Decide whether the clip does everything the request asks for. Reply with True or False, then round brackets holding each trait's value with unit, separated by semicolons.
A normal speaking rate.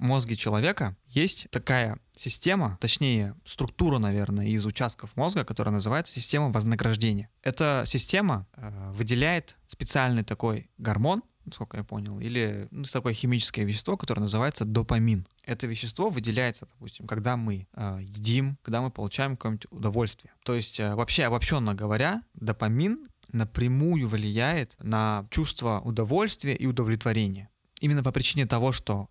True (135 wpm)